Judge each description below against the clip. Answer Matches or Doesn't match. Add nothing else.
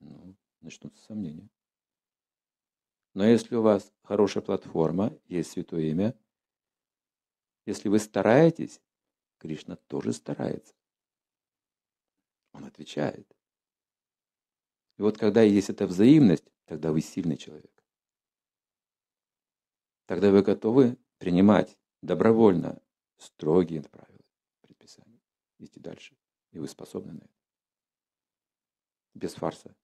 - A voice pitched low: Matches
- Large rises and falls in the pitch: Doesn't match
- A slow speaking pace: Matches